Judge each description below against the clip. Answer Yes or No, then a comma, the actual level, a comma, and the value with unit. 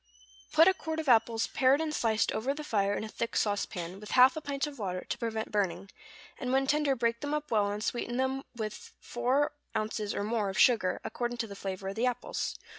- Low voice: No, high, 230 Hz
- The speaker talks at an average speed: No, fast, 235 wpm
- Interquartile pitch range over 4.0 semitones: Yes, average, 4.5 semitones